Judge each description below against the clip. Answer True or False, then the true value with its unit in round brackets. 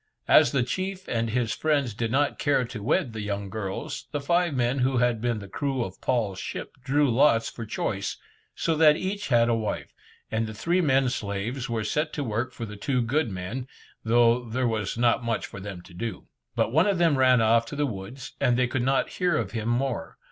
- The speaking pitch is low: True (120 Hz)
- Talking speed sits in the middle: False (220 wpm)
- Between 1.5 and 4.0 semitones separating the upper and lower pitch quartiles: True (3.7 semitones)